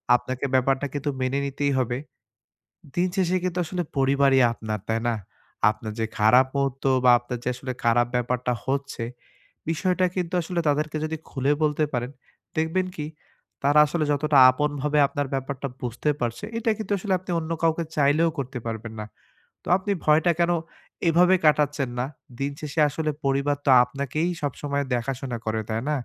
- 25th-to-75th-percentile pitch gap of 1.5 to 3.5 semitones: No, average, 3.9 semitones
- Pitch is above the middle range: No, medium, 140 Hz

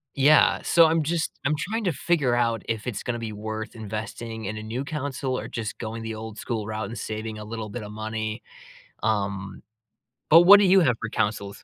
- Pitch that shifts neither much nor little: Yes, average, 4.4 semitones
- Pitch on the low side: Yes, low, 115 Hz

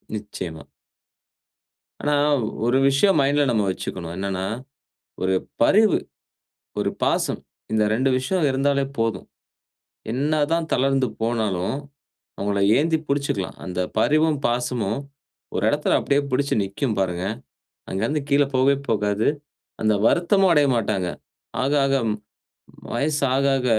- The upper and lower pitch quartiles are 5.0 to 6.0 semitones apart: Yes, wide, 5.5 semitones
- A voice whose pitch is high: No, low, 130 Hz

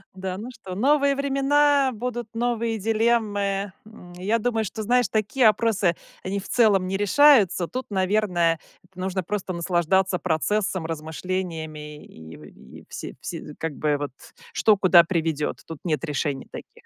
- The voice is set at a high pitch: Yes, high, 195 Hz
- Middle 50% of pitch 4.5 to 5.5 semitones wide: Yes, average, 4.8 semitones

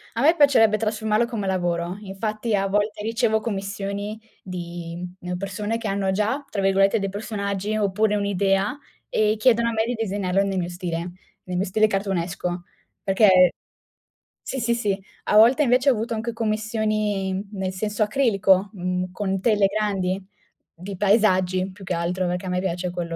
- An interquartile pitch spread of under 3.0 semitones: Yes, narrow, 2.6 semitones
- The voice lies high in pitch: Yes, high, 200 Hz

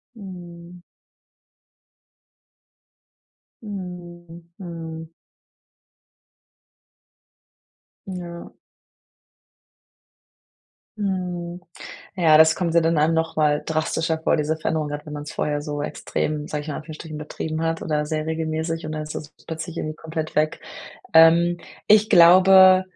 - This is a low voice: No, medium, 160 Hz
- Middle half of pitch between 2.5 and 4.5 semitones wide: No, narrow, 2.0 semitones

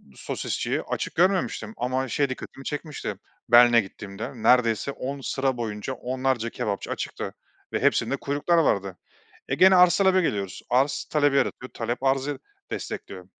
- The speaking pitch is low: Yes, low, 130 Hz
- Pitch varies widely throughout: No, average, 3.7 semitones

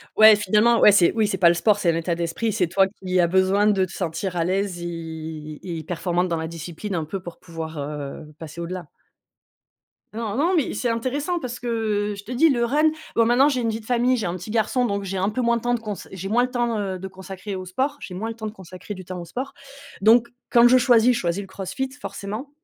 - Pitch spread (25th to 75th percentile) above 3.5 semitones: Yes, average, 5.1 semitones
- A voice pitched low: No, high, 200 Hz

